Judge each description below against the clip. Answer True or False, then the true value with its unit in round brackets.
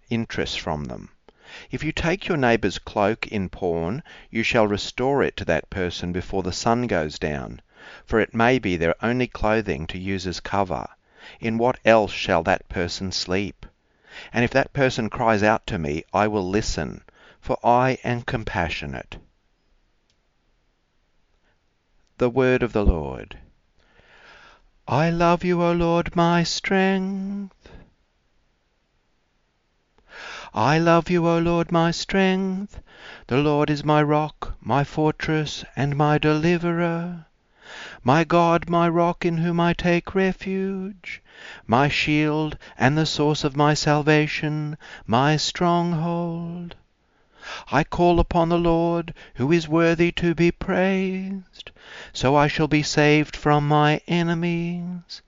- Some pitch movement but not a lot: False (8.2 semitones)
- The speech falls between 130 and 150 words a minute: True (135 wpm)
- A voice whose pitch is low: False (150 Hz)